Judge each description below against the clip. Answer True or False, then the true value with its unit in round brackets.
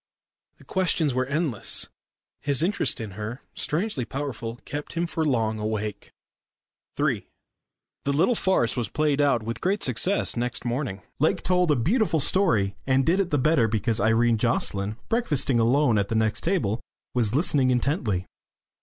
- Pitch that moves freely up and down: True (5.9 semitones)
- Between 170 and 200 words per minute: False (155 wpm)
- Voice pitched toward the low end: True (130 Hz)